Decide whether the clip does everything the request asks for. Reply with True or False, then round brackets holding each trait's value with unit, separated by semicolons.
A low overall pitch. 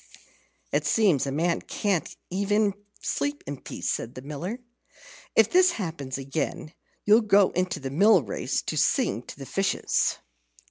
False (175 Hz)